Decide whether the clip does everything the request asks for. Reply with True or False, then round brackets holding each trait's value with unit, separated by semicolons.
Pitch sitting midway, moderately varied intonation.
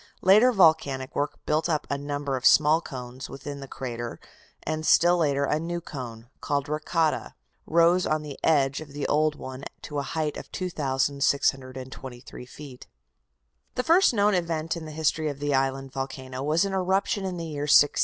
True (145 Hz; 3.4 semitones)